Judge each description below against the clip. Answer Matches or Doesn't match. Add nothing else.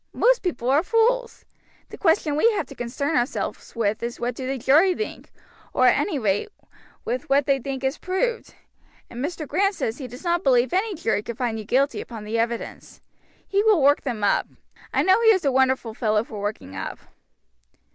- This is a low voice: Doesn't match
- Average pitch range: Doesn't match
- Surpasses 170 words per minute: Matches